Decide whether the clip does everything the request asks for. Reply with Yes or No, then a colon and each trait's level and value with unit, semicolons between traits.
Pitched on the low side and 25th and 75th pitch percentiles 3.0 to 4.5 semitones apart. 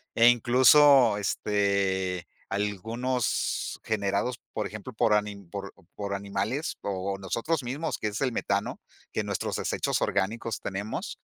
Yes: low, 105 Hz; average, 3.5 semitones